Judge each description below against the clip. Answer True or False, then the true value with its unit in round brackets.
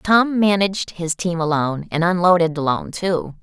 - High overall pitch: False (175 Hz)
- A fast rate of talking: False (160 wpm)